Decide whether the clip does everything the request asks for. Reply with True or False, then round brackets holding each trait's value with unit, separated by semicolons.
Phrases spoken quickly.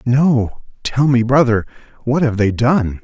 False (160 wpm)